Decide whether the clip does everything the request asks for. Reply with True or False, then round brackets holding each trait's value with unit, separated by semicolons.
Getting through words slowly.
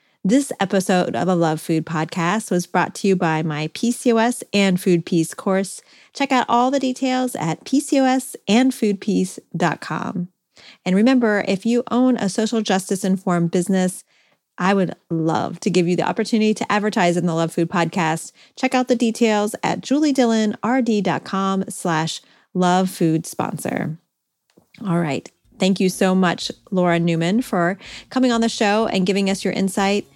False (155 wpm)